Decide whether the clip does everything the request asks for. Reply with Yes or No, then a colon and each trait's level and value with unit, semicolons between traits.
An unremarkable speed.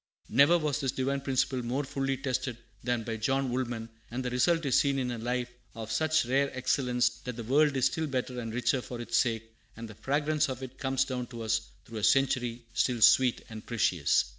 No: fast, 215 wpm